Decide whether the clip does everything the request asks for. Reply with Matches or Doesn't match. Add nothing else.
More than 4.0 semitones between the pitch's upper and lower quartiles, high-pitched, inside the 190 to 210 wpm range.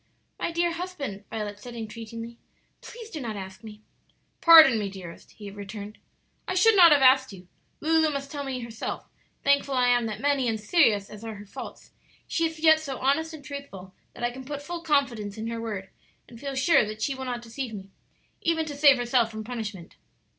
Matches